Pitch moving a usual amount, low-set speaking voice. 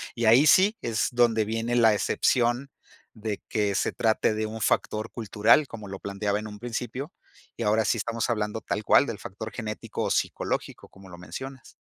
No: narrow, 2.3 semitones; low, 110 Hz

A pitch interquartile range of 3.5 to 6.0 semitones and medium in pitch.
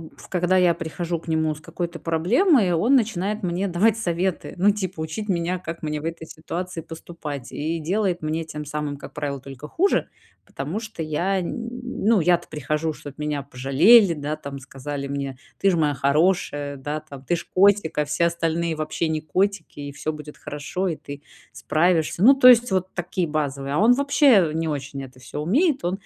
Yes: average, 4.0 semitones; medium, 165 Hz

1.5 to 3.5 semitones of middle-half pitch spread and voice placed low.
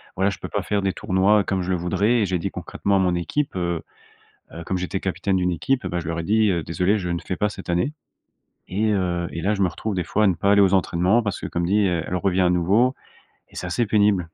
Yes: average, 2.7 semitones; very low, 95 Hz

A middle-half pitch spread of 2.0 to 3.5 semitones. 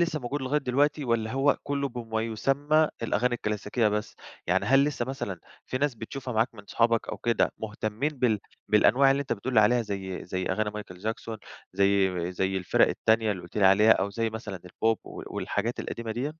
No: average, 4.0 semitones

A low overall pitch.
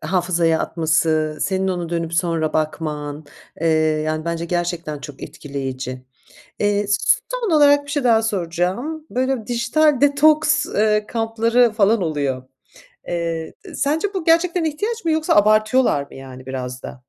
No: high, 190 Hz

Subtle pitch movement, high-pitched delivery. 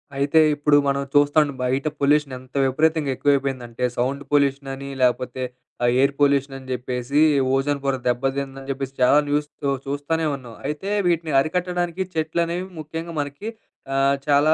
No: narrow, 2.1 semitones; medium, 140 Hz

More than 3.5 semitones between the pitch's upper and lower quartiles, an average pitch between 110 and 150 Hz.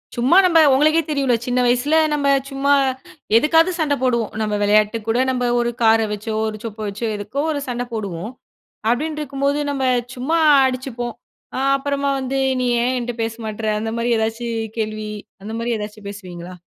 No: average, 4.1 semitones; high, 240 Hz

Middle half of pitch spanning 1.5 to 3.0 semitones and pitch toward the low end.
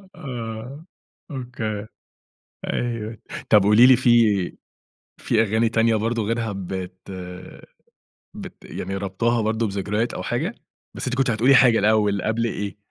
Yes: narrow, 2.4 semitones; low, 110 Hz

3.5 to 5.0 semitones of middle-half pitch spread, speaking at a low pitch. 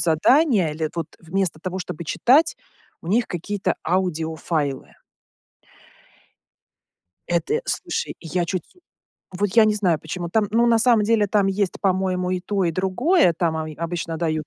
No: average, 4.2 semitones; medium, 185 Hz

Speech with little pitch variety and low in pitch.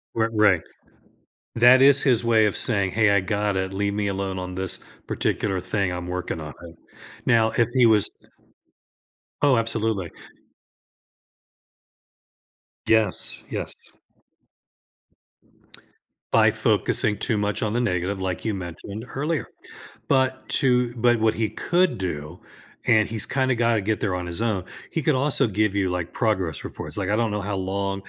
No: average, 3.7 semitones; low, 105 Hz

